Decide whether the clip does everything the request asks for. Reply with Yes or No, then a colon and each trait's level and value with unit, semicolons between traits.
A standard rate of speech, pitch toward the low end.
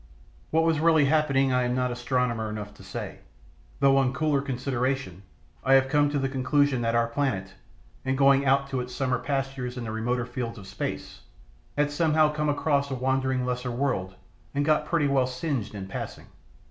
Yes: average, 185 wpm; low, 130 Hz